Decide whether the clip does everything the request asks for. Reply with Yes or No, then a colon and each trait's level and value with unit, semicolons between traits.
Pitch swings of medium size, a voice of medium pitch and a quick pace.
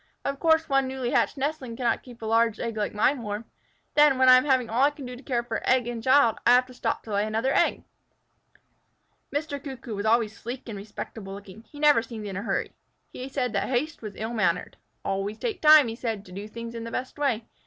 No: average, 3.5 semitones; high, 235 Hz; fast, 240 wpm